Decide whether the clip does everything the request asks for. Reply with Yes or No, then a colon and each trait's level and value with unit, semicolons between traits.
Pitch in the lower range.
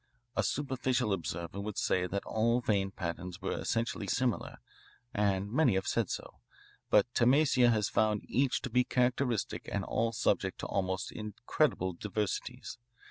Yes: low, 105 Hz